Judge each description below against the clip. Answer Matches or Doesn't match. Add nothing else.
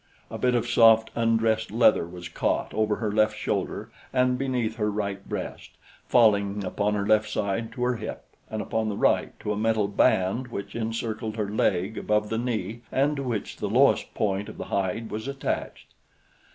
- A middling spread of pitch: Doesn't match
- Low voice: Matches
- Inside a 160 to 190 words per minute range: Matches